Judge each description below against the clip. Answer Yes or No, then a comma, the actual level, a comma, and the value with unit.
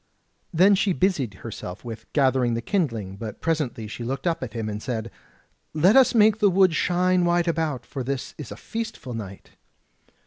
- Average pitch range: No, wide, 7.9 semitones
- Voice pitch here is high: No, medium, 140 Hz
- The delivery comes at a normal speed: Yes, average, 180 wpm